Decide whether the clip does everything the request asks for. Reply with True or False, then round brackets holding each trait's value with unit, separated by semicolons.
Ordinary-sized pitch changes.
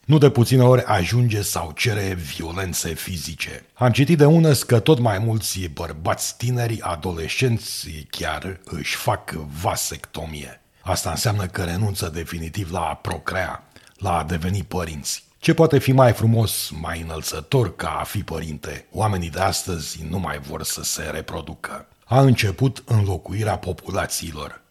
False (5.7 semitones)